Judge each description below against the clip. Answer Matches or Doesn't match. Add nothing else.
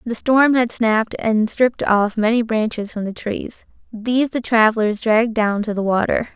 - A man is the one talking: Doesn't match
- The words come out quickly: Doesn't match